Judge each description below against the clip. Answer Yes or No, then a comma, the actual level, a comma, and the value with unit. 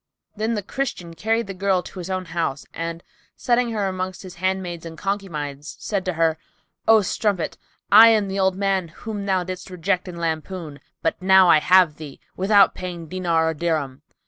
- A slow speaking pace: No, average, 185 wpm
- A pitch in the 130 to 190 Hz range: Yes, medium, 185 Hz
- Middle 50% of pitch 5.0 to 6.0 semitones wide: No, average, 3.0 semitones